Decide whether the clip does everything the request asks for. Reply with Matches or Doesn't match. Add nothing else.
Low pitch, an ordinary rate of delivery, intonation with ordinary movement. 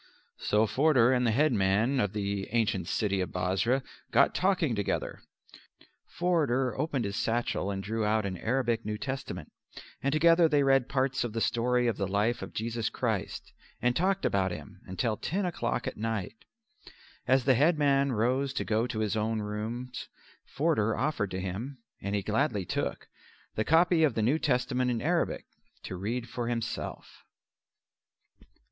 Matches